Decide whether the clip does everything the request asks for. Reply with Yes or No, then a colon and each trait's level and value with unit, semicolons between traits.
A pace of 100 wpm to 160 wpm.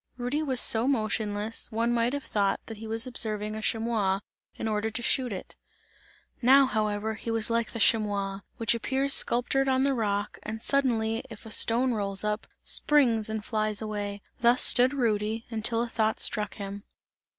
No: average, 175 wpm